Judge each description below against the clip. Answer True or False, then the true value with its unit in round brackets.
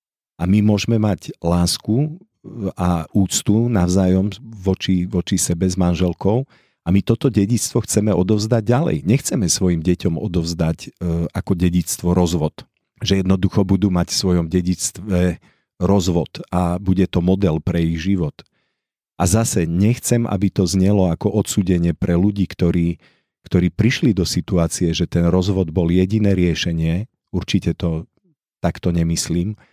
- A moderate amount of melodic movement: True (3.1 semitones)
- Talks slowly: False (135 wpm)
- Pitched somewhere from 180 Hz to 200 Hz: False (95 Hz)